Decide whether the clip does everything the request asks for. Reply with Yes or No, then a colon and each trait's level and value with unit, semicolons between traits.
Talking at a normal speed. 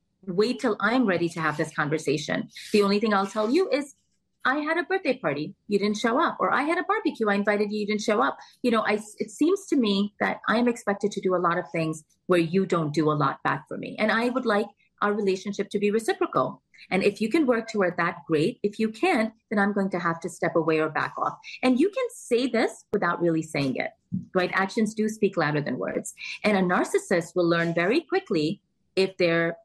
No: fast, 235 wpm